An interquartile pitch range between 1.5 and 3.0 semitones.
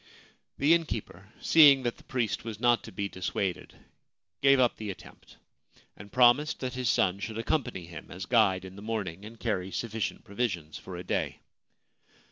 No: average, 4.6 semitones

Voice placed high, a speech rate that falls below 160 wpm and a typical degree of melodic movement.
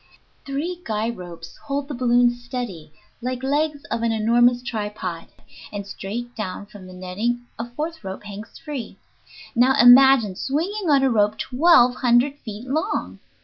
Yes: high, 240 Hz; average, 150 wpm; average, 4.4 semitones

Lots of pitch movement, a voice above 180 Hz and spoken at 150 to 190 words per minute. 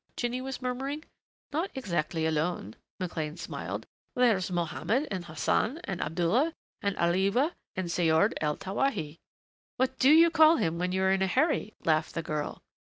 Yes: wide, 7.8 semitones; high, 190 Hz; average, 165 wpm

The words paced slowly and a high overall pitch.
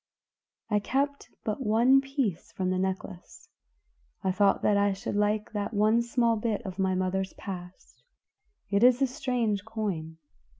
No: average, 155 wpm; high, 210 Hz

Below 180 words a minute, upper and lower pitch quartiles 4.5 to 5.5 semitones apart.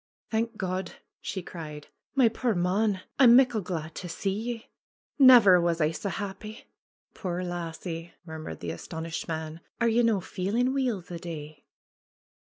Yes: average, 160 wpm; average, 5.2 semitones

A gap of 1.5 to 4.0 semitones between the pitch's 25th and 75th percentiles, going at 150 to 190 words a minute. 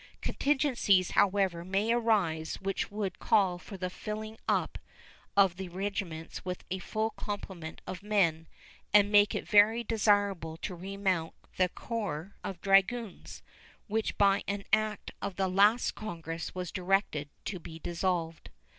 No: average, 2.9 semitones; average, 140 wpm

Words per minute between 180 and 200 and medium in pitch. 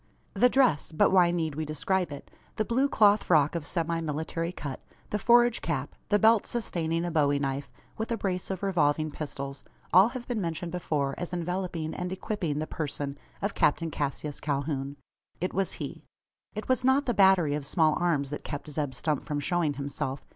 Yes: average, 190 wpm; medium, 165 Hz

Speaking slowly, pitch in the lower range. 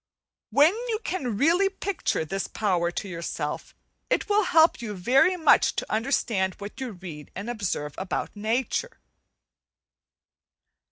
No: slow, 130 wpm; high, 220 Hz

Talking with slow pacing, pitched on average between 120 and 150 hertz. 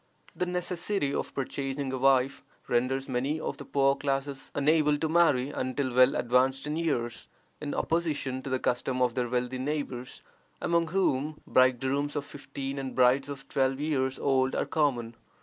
No: average, 165 wpm; low, 135 Hz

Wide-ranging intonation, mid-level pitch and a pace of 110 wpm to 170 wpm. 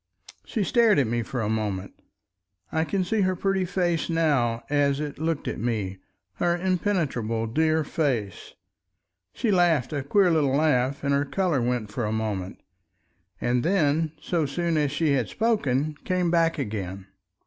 Yes: wide, 6.5 semitones; medium, 145 Hz; average, 160 wpm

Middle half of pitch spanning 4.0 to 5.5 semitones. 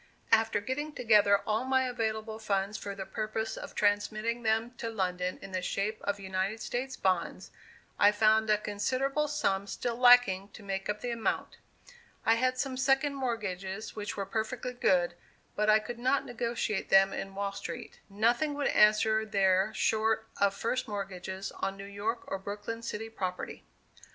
No: average, 3.1 semitones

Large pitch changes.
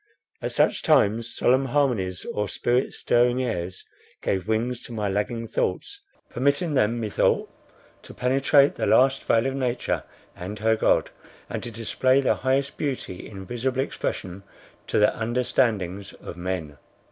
No: average, 4.3 semitones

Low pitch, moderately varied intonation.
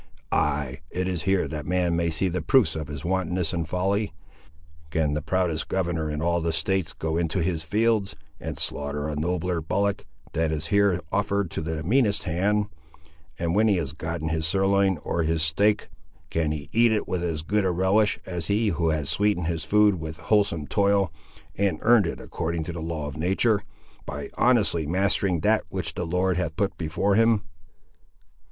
Yes: very low, 85 Hz; average, 3.9 semitones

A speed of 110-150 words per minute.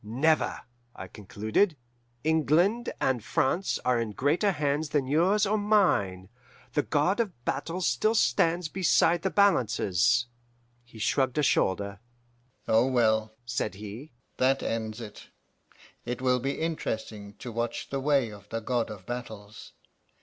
Yes: average, 140 wpm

